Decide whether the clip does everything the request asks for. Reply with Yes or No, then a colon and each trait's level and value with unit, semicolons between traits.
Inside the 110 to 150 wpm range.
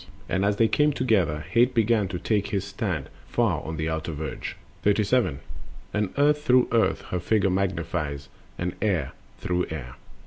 No: average, 175 wpm